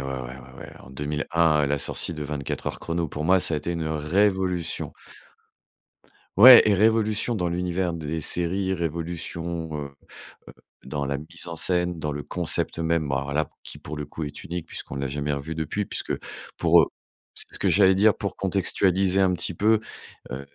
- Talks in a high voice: No, very low, 85 Hz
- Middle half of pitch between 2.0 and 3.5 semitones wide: No, average, 4.0 semitones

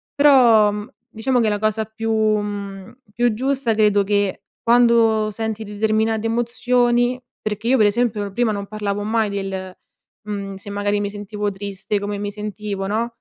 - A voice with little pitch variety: Yes, narrow, 2.1 semitones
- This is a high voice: Yes, high, 215 Hz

